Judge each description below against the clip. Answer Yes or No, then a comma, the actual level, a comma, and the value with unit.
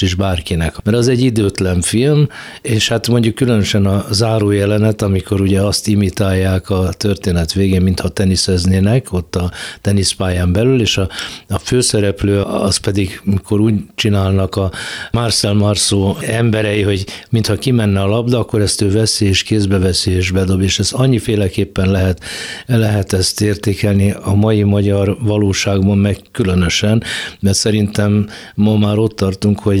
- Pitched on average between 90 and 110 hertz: Yes, low, 100 Hz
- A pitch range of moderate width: No, narrow, 2.1 semitones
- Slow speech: No, average, 150 wpm